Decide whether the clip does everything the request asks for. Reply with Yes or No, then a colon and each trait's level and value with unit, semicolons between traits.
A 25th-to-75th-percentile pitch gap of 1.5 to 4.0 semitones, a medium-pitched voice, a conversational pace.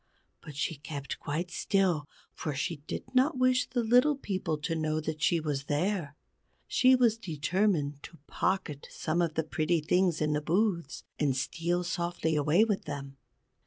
No: average, 4.4 semitones; medium, 165 Hz; average, 165 wpm